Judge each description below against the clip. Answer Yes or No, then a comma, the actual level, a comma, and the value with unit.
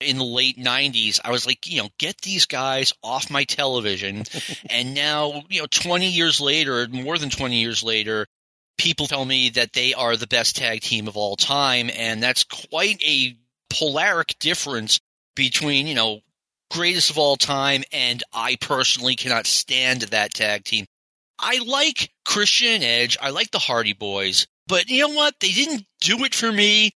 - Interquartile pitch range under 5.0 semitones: No, wide, 5.6 semitones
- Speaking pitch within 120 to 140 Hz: Yes, low, 135 Hz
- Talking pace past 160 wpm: Yes, average, 180 wpm